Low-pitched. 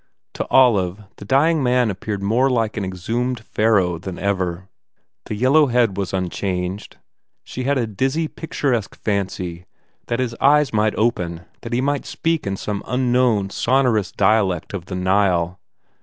Yes: low, 105 Hz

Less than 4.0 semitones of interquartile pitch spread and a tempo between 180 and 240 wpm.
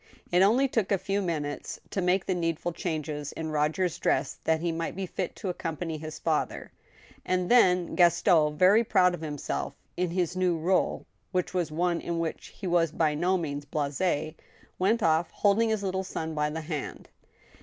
Yes: average, 2.8 semitones; average, 185 wpm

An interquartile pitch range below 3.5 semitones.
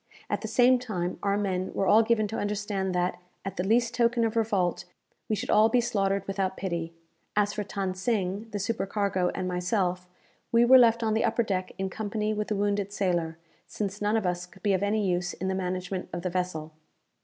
Yes: average, 2.9 semitones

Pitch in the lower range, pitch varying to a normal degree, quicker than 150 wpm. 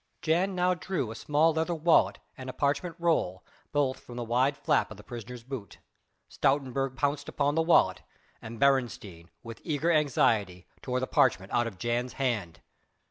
Yes: low, 130 Hz; average, 4.6 semitones; average, 170 wpm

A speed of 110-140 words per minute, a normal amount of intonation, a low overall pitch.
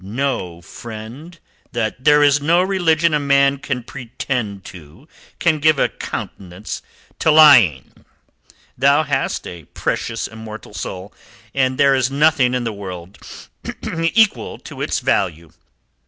No: slow, 135 wpm; wide, 6.0 semitones; low, 130 Hz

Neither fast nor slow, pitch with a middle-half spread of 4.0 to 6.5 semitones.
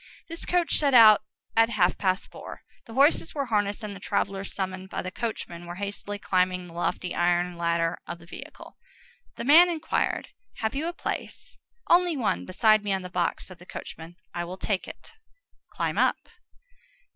Yes: average, 180 wpm; average, 4.7 semitones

